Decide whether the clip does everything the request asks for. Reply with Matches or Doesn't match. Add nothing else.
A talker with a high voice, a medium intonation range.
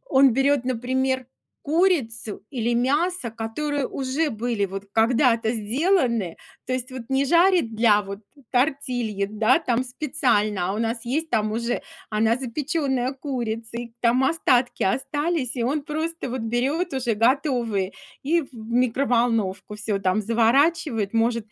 Matches